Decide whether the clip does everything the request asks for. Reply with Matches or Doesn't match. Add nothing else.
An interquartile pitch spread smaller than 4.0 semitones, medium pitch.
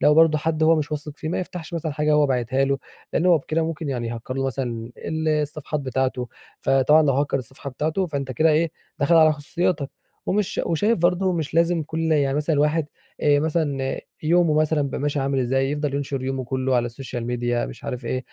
Matches